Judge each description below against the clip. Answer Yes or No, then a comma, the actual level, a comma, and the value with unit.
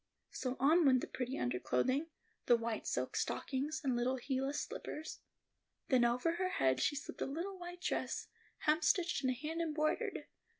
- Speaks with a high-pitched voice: Yes, very high, 275 Hz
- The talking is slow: No, average, 160 wpm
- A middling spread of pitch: Yes, average, 4.3 semitones